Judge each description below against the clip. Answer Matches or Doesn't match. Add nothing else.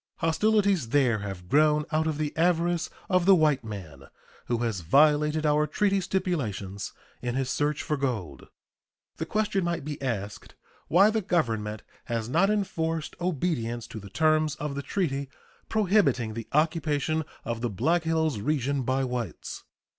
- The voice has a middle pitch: Matches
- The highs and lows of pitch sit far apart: Matches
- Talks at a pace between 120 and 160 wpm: Matches